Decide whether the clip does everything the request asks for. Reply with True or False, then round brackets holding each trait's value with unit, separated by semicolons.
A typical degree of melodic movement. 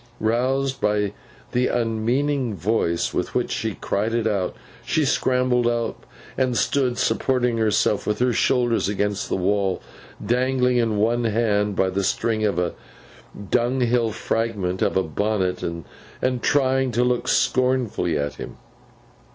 True (3.5 semitones)